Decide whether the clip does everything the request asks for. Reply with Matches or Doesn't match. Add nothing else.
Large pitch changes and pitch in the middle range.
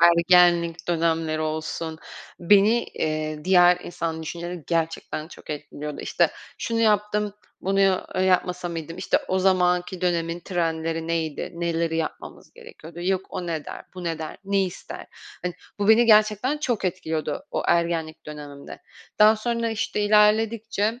Doesn't match